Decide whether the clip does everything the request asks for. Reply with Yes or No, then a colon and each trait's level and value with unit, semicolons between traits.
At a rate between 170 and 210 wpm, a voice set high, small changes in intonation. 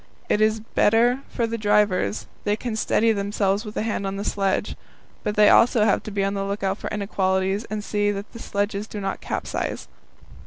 Yes: average, 200 wpm; high, 205 Hz; narrow, 1.5 semitones